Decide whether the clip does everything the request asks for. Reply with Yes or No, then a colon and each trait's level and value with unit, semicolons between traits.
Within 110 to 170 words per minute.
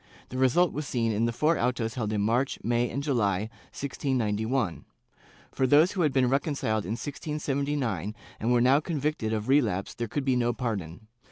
No: average, 180 wpm